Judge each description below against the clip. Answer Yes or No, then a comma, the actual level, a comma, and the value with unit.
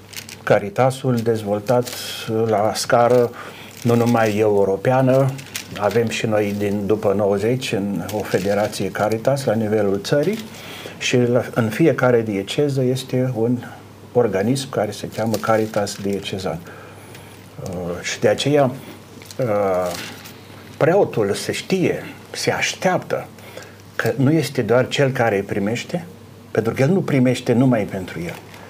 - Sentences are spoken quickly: No, average, 120 wpm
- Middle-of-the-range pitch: No, low, 115 Hz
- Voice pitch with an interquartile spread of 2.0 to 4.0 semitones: Yes, average, 3.5 semitones